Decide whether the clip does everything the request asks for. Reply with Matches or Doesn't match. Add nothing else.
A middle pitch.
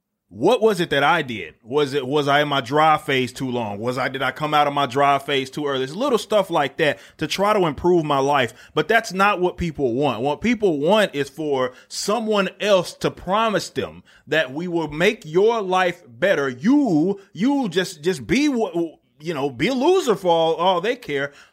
Matches